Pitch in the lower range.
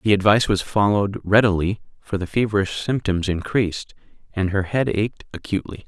Yes: low, 100 Hz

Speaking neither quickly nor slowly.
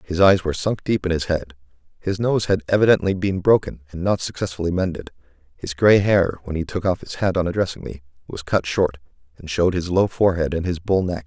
No: fast, 225 wpm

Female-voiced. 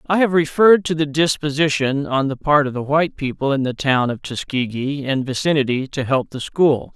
No: male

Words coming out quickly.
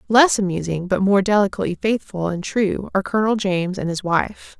No: average, 185 wpm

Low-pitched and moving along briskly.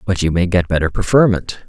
Yes: very low, 95 Hz; fast, 215 wpm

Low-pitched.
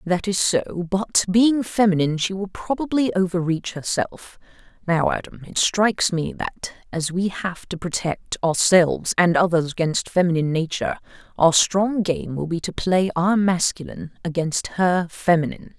No: medium, 180 Hz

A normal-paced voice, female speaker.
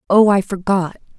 Yes: average, 150 wpm; female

